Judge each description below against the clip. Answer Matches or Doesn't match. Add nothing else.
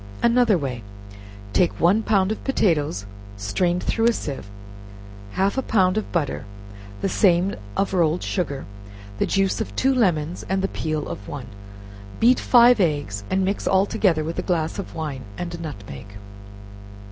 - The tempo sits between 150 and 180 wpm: Matches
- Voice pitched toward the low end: Doesn't match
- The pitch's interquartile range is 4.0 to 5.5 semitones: Matches